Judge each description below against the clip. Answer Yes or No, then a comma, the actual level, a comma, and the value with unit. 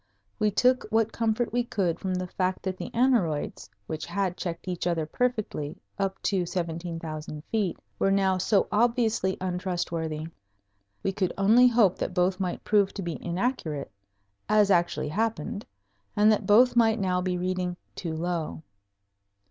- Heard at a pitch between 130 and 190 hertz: Yes, medium, 185 Hz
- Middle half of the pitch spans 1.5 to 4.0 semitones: Yes, average, 3.7 semitones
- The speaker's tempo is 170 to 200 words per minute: No, average, 155 wpm